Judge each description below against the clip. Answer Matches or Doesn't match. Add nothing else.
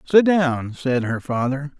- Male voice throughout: Matches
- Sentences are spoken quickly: Doesn't match